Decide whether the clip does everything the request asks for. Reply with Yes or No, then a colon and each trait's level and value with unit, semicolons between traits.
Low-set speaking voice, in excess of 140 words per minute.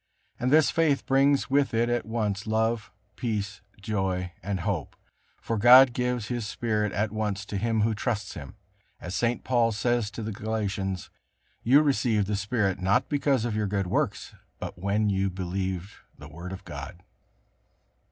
Yes: low, 105 Hz; average, 165 wpm